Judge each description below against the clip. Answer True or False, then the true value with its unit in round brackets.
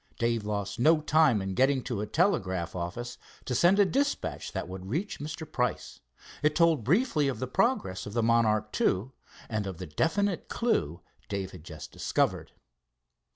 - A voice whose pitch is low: True (120 Hz)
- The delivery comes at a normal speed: True (170 wpm)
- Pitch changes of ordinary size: False (8.7 semitones)